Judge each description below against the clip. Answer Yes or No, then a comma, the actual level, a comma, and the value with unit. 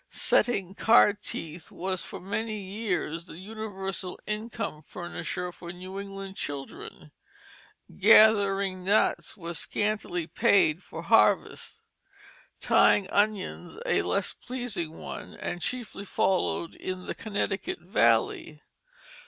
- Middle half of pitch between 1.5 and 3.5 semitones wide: Yes, average, 3.2 semitones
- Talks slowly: Yes, slow, 110 wpm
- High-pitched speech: Yes, high, 195 Hz